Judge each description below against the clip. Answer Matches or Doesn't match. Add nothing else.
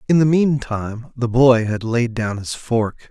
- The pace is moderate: Matches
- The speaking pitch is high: Doesn't match